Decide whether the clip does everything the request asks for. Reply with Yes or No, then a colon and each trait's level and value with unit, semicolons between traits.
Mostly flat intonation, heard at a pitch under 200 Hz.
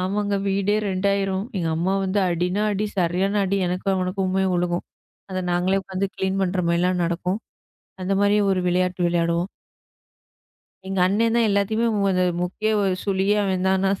Yes: narrow, 1.5 semitones; high, 190 Hz